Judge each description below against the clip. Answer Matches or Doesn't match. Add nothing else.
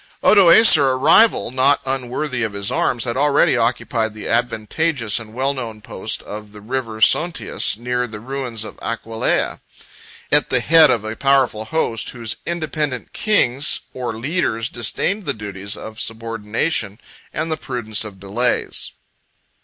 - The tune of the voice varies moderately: Matches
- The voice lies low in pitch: Matches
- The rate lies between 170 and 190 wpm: Doesn't match